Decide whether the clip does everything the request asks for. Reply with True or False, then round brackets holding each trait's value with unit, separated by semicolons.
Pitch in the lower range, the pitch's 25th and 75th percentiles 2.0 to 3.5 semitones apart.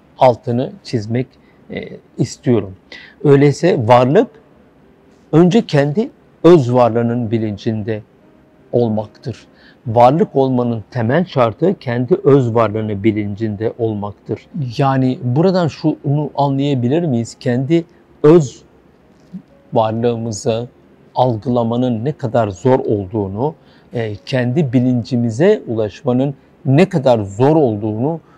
False (125 Hz; 4.0 semitones)